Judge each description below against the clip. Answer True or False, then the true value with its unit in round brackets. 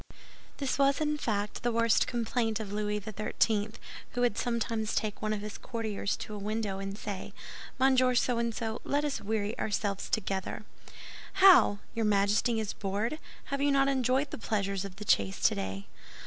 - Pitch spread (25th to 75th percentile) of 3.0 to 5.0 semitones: True (3.3 semitones)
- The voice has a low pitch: False (220 Hz)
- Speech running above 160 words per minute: True (175 wpm)